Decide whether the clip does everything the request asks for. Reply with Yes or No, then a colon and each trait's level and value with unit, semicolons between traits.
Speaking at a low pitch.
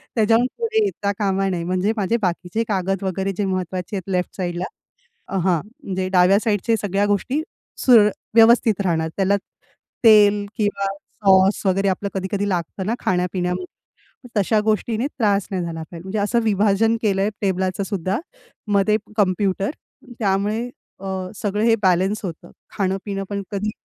No: high, 195 Hz